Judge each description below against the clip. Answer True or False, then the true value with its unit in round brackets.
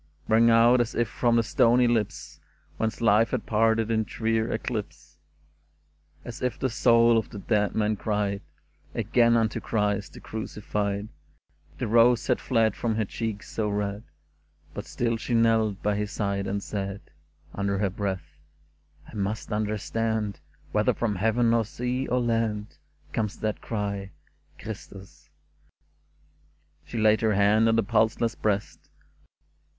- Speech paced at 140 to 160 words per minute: True (155 wpm)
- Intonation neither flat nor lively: False (2.1 semitones)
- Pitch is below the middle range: True (110 Hz)